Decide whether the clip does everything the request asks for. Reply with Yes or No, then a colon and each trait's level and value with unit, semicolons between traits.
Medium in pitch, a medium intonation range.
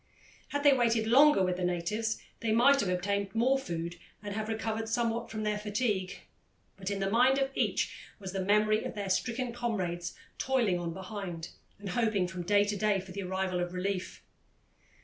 No: high, 205 Hz; average, 3.5 semitones